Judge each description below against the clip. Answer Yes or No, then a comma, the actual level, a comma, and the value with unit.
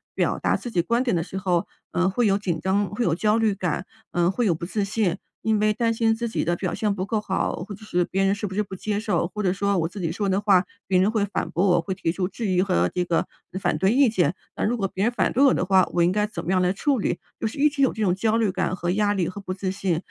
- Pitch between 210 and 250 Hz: No, high, 195 Hz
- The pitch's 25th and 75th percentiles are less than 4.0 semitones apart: Yes, average, 2.9 semitones